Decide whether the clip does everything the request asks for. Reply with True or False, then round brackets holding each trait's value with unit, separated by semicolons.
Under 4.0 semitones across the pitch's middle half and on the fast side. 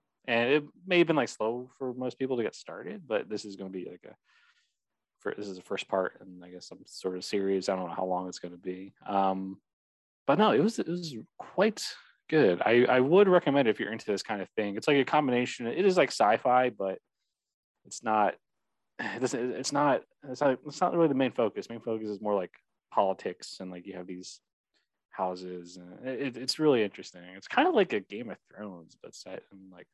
False (5.5 semitones; 235 wpm)